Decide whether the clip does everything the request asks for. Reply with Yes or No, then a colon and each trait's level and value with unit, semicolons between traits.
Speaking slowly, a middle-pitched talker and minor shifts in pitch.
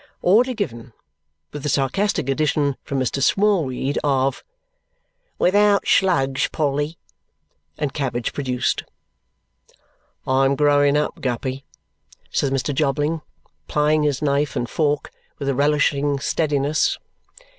Yes: slow, 115 wpm; medium, 145 Hz; narrow, 2.1 semitones